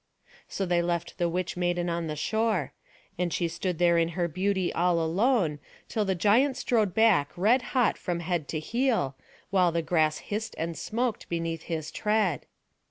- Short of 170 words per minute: No, average, 175 wpm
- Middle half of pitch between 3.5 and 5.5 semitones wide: Yes, average, 4.0 semitones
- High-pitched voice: No, medium, 175 Hz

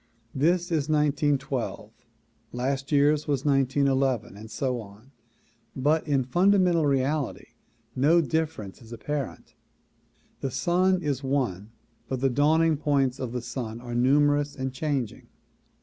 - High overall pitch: No, medium, 140 Hz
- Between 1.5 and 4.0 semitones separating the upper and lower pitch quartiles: Yes, average, 3.0 semitones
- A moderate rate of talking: No, slow, 125 wpm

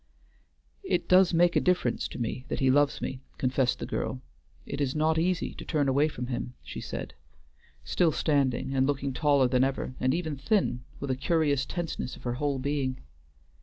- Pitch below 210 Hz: Yes, medium, 140 Hz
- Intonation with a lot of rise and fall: No, average, 3.2 semitones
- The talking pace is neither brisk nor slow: Yes, average, 190 wpm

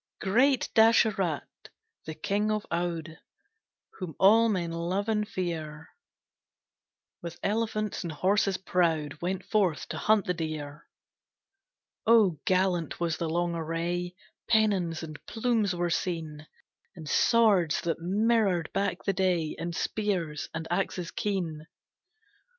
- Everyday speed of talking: No, slow, 120 wpm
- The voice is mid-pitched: Yes, medium, 180 Hz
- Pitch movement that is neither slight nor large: Yes, average, 3.9 semitones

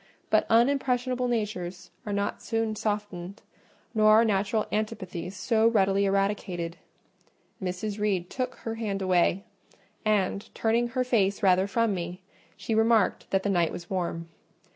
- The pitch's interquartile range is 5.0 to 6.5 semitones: No, average, 3.3 semitones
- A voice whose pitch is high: Yes, high, 205 Hz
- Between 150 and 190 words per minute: No, average, 140 wpm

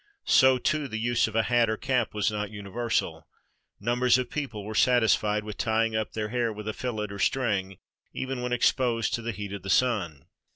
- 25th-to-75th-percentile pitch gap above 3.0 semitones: No, average, 2.7 semitones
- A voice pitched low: Yes, low, 110 Hz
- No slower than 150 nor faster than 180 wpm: No, fast, 205 wpm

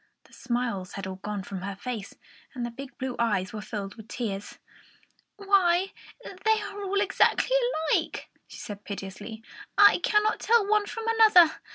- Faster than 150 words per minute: Yes, average, 165 wpm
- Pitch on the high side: Yes, high, 245 Hz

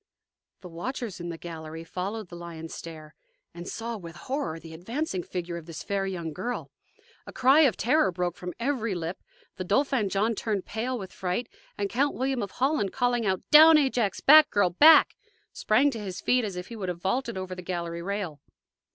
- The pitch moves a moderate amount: No, wide, 6.0 semitones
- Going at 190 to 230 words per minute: Yes, average, 195 wpm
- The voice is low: No, high, 195 Hz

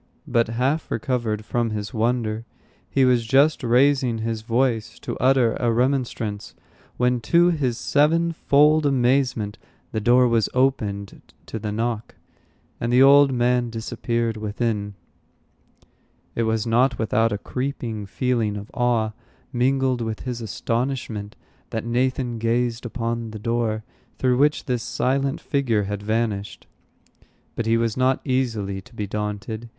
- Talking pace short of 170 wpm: Yes, slow, 135 wpm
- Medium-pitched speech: No, low, 120 Hz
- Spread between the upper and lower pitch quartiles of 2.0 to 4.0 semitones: Yes, average, 2.7 semitones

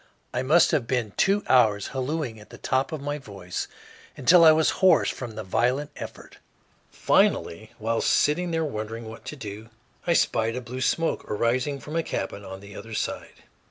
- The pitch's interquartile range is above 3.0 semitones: Yes, wide, 5.5 semitones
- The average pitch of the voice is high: No, low, 125 Hz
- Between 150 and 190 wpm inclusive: Yes, average, 185 wpm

